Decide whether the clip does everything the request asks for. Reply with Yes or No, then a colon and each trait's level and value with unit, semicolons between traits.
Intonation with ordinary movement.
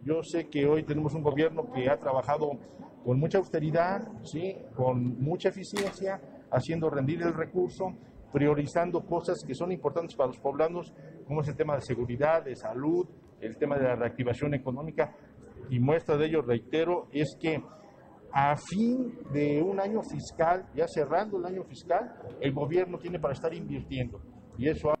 Yes: average, 3.7 semitones